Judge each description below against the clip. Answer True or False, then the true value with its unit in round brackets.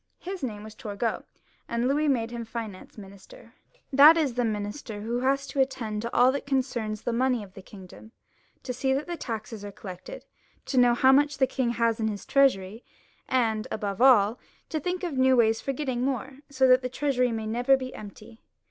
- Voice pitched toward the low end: False (245 Hz)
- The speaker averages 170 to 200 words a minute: True (195 wpm)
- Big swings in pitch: False (3.6 semitones)